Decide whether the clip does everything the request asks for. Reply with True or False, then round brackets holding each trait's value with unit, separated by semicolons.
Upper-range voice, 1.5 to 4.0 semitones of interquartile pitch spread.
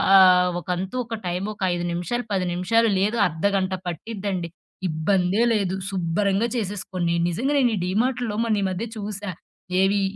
True (195 Hz; 2.9 semitones)